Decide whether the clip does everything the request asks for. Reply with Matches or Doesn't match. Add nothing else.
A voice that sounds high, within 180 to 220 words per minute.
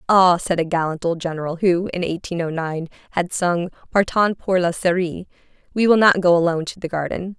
Doesn't match